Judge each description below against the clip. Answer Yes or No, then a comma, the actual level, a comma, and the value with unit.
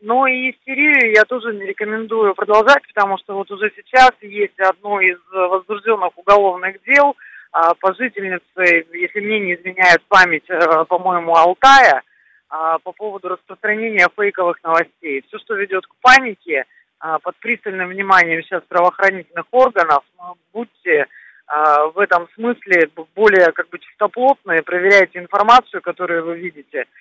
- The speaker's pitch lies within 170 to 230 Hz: Yes, high, 190 Hz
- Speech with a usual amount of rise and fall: Yes, average, 3.6 semitones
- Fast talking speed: No, average, 125 wpm